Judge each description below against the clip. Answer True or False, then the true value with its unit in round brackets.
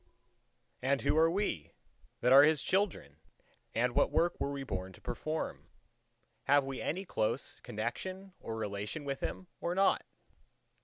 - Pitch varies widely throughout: True (7.1 semitones)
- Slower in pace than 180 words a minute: True (150 wpm)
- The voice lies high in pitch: False (140 Hz)